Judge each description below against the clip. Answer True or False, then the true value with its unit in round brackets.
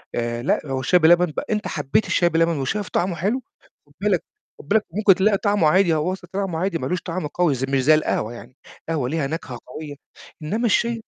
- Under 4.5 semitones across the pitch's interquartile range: False (5.1 semitones)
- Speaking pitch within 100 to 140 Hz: False (165 Hz)